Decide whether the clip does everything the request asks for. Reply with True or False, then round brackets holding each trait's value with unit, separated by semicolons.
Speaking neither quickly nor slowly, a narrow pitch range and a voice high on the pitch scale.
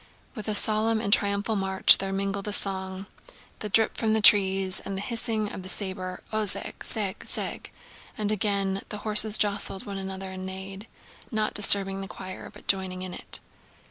True (175 wpm; 1.8 semitones; 200 Hz)